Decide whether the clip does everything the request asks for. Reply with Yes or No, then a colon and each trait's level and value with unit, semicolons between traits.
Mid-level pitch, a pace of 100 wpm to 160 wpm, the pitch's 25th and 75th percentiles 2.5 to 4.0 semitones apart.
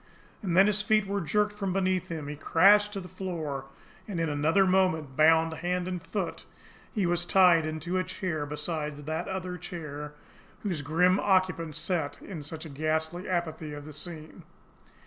No: medium, 170 Hz; average, 170 wpm; average, 3.2 semitones